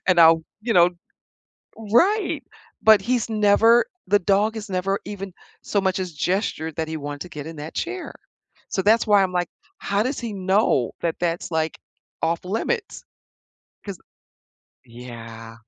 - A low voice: No, high, 190 Hz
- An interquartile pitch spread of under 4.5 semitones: No, average, 4.8 semitones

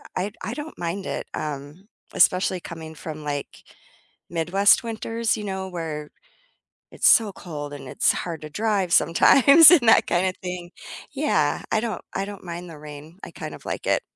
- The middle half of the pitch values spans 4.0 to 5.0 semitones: Yes, average, 4.6 semitones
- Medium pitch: Yes, medium, 180 Hz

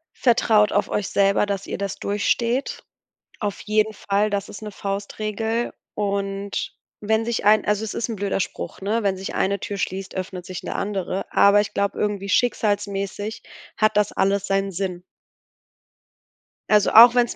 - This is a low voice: No, high, 205 Hz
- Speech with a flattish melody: Yes, narrow, 1.4 semitones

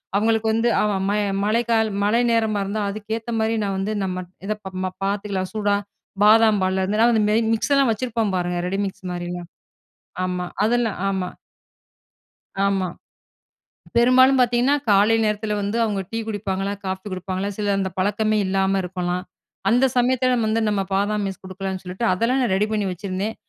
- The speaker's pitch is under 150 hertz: No, high, 205 Hz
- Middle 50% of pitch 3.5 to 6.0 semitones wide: No, average, 2.9 semitones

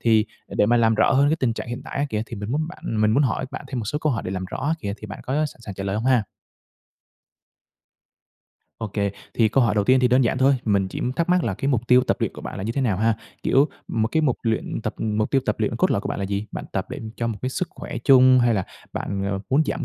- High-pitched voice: No, low, 115 Hz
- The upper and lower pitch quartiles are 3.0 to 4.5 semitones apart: Yes, average, 3.9 semitones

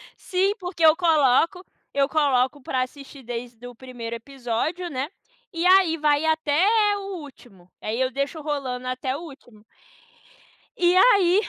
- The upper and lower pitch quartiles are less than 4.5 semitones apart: No, average, 4.8 semitones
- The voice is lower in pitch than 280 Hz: No, very high, 285 Hz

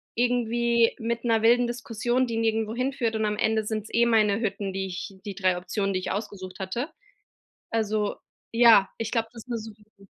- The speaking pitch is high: Yes, high, 225 Hz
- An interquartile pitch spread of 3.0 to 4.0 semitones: No, narrow, 2.4 semitones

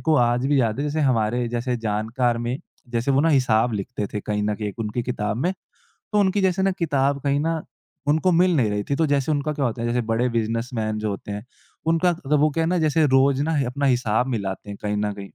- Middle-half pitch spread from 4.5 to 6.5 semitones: Yes, average, 5.2 semitones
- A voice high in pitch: No, low, 125 Hz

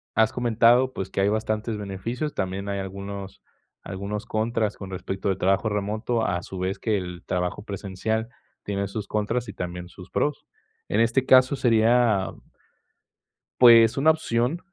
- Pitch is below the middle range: Yes, low, 105 Hz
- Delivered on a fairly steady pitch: No, average, 3.2 semitones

